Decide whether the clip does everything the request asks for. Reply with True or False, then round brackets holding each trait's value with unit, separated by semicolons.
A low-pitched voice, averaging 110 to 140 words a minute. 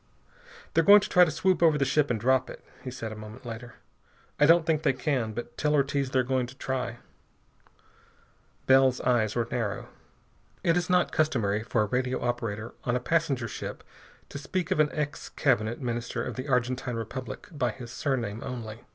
False (130 Hz; 190 wpm)